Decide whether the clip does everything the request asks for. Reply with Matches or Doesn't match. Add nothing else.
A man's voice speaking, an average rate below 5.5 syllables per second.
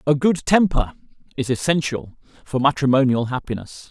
Matches